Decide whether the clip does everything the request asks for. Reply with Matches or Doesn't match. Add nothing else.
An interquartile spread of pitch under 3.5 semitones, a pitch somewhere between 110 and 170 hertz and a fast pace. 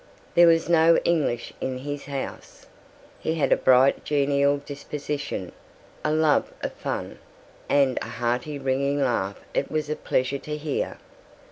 Doesn't match